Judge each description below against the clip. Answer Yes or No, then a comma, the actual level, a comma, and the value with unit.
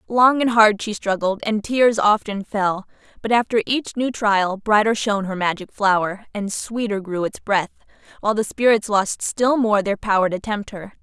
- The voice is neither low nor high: No, high, 210 Hz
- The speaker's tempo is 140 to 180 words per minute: No, average, 190 wpm